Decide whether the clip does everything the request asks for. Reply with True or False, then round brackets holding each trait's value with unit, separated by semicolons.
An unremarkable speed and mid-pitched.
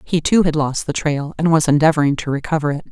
False (245 wpm; 150 Hz)